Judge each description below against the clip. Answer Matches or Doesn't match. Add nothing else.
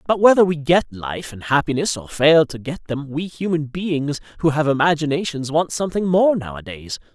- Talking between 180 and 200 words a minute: Matches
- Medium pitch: Matches